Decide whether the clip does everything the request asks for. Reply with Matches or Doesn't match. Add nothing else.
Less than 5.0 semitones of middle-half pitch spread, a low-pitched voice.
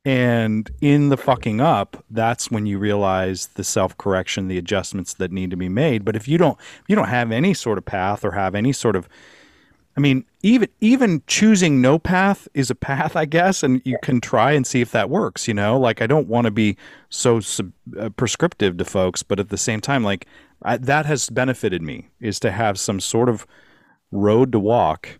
Doesn't match